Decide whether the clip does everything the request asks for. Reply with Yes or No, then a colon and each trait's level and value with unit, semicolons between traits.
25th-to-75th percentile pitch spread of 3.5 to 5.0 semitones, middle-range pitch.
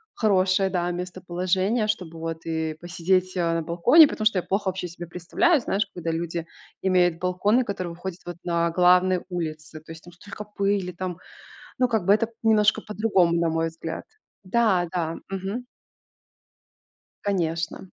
No: average, 3.0 semitones; medium, 180 Hz